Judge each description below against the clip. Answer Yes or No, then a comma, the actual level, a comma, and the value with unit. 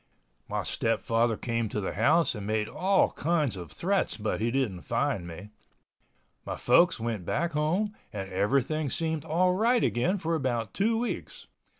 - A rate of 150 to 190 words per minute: Yes, average, 165 wpm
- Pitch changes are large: Yes, wide, 7.7 semitones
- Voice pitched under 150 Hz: Yes, low, 135 Hz